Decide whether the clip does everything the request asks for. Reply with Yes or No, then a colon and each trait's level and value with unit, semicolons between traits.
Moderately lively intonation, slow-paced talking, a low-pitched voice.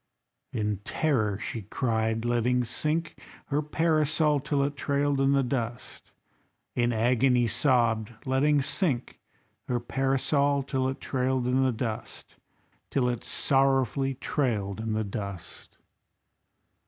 Yes: average, 3.4 semitones; slow, 120 wpm; low, 130 Hz